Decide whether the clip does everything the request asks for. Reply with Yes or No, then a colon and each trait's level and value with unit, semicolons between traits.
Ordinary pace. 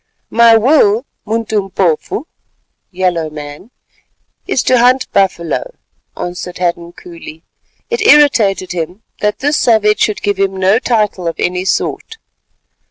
No: slow, 120 wpm